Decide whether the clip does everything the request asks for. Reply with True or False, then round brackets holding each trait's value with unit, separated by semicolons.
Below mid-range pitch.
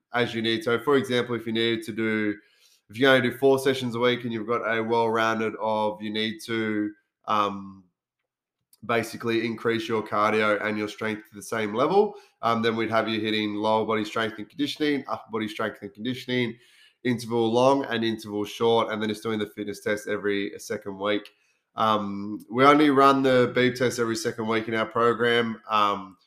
True (115 Hz)